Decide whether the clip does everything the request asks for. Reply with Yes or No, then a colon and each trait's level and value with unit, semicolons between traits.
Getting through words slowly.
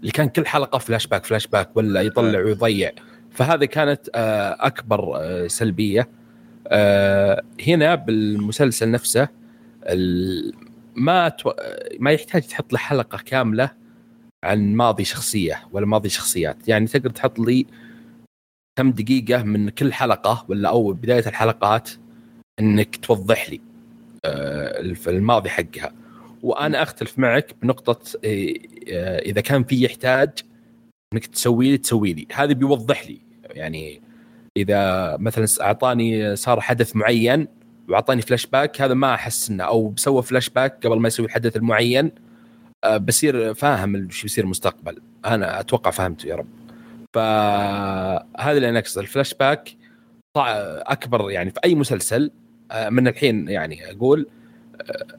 No: average, 120 wpm